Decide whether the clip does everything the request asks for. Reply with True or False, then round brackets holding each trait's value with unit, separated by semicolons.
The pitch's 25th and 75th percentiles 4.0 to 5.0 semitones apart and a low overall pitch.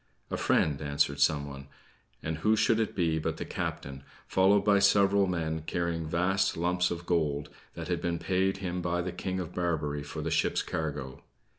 False (3.5 semitones; 85 Hz)